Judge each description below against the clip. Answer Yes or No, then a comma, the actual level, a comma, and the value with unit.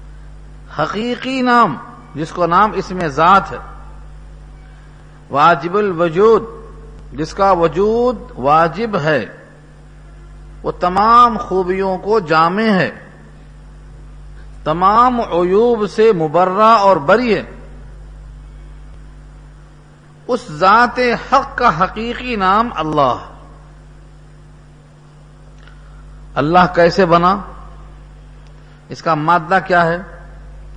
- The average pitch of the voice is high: No, medium, 175 Hz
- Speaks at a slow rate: Yes, slow, 85 wpm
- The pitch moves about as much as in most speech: No, wide, 6.1 semitones